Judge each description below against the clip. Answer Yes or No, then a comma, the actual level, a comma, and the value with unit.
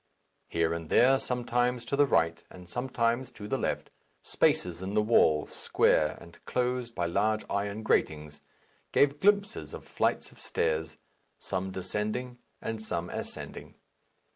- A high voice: No, low, 105 Hz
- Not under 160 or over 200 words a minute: No, average, 140 wpm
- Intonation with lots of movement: Yes, wide, 6.6 semitones